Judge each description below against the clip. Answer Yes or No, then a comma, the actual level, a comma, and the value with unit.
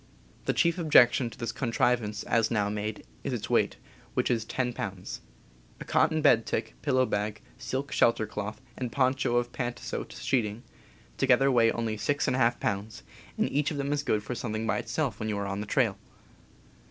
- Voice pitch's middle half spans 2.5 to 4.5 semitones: Yes, average, 3.5 semitones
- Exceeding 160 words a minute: Yes, average, 180 wpm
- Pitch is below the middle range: Yes, low, 120 Hz